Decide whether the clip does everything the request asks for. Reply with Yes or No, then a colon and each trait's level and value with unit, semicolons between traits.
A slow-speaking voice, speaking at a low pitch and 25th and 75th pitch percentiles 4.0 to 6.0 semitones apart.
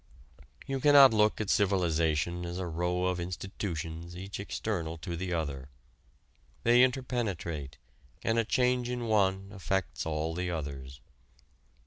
Yes: slow, 130 wpm; very low, 90 Hz; average, 4.8 semitones